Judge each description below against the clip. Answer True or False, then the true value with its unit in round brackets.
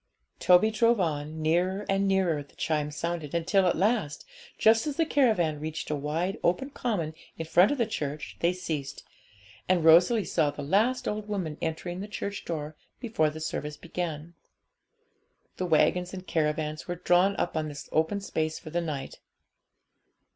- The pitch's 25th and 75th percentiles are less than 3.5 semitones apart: False (4.2 semitones)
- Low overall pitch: False (170 Hz)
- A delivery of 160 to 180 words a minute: True (170 wpm)